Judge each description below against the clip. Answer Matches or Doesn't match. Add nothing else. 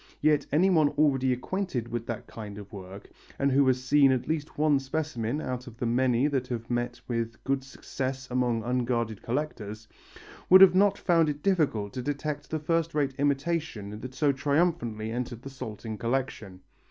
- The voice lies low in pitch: Matches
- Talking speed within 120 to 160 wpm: Doesn't match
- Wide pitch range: Doesn't match